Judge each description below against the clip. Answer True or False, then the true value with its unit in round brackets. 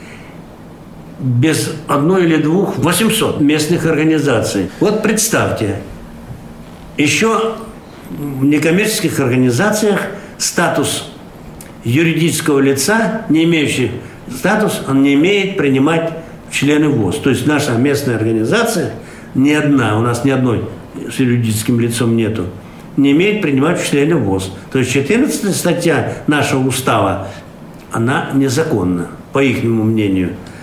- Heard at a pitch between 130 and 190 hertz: True (140 Hz)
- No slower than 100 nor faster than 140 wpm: True (115 wpm)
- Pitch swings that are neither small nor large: False (6.1 semitones)